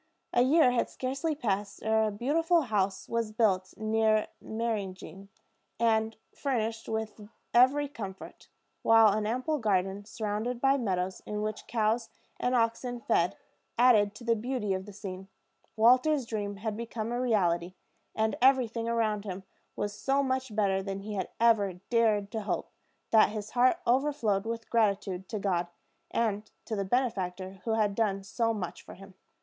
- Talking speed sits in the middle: Yes, average, 160 wpm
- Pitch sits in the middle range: No, high, 220 Hz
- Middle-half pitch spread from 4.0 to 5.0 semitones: No, average, 2.9 semitones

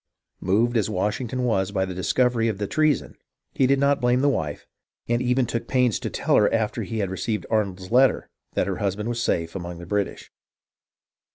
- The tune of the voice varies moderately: Yes, average, 4.5 semitones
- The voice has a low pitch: Yes, low, 110 Hz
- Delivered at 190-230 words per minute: Yes, average, 195 wpm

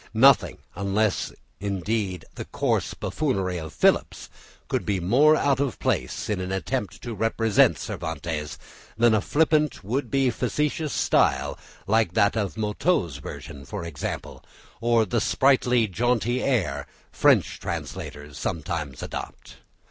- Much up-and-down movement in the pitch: Yes, wide, 5.9 semitones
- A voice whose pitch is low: Yes, low, 105 Hz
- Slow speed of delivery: Yes, slow, 130 wpm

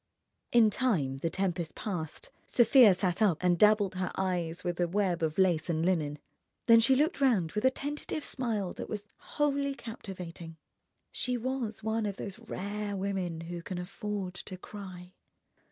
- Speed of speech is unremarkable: Yes, average, 165 wpm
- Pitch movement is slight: No, average, 4.2 semitones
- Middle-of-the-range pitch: No, high, 195 Hz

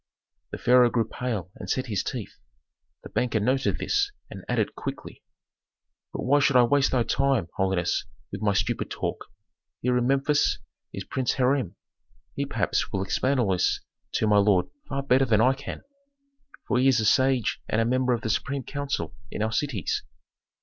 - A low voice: Yes, low, 125 Hz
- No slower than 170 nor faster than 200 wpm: Yes, average, 180 wpm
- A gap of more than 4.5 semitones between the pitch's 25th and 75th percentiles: No, average, 3.9 semitones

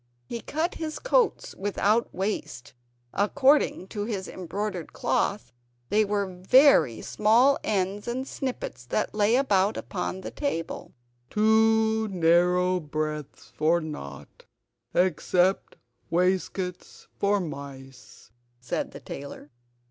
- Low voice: No, high, 190 Hz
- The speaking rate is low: Yes, slow, 110 wpm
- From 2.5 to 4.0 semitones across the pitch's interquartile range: No, average, 4.8 semitones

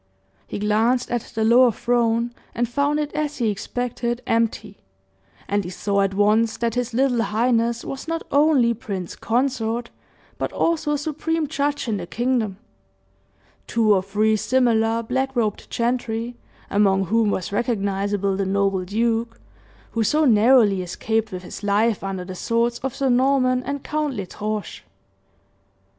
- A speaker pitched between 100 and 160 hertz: No, high, 230 Hz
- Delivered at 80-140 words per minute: No, average, 150 wpm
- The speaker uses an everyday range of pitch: Yes, average, 3.5 semitones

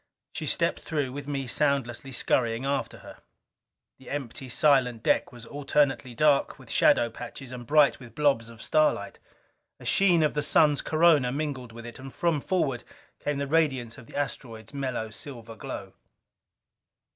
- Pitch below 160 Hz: Yes, low, 135 Hz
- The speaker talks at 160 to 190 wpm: Yes, average, 165 wpm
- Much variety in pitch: No, average, 3.5 semitones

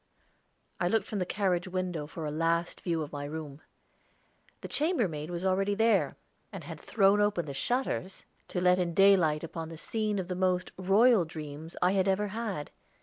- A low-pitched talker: No, medium, 180 Hz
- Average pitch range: Yes, average, 3.6 semitones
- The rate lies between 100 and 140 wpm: No, average, 185 wpm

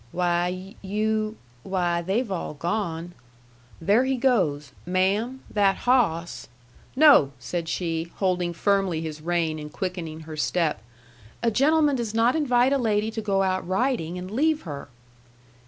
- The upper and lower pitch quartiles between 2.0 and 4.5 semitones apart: No, average, 5.1 semitones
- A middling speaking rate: Yes, average, 145 wpm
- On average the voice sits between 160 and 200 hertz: Yes, high, 190 Hz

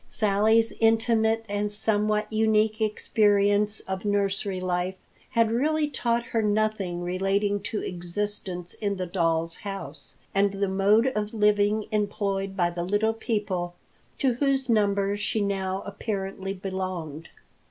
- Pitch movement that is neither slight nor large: No, narrow, 2.2 semitones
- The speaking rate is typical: No, slow, 130 wpm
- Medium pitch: No, high, 205 Hz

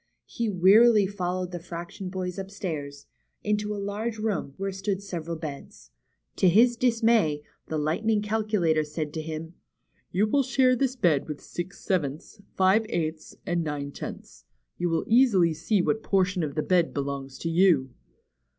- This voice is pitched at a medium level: Yes, medium, 180 Hz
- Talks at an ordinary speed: Yes, average, 160 wpm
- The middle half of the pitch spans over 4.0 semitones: Yes, average, 5.0 semitones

